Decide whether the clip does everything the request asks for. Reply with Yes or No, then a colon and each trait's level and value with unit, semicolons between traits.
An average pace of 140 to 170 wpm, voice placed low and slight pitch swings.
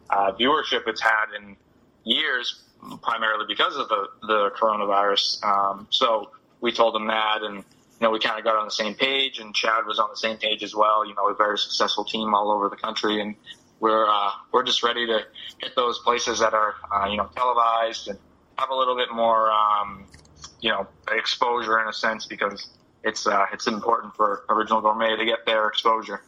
No: fast, 205 wpm; low, 110 Hz; narrow, 1.7 semitones